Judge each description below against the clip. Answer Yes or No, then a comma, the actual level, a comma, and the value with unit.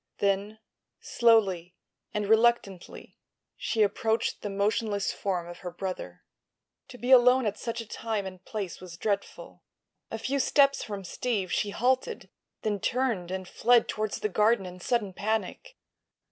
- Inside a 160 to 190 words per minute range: No, average, 145 wpm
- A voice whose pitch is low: No, high, 210 Hz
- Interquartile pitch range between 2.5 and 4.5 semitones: Yes, average, 3.5 semitones